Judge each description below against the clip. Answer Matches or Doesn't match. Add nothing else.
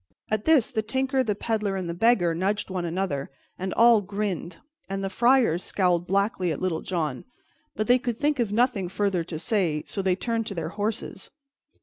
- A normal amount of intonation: Matches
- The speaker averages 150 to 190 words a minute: Doesn't match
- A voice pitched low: Doesn't match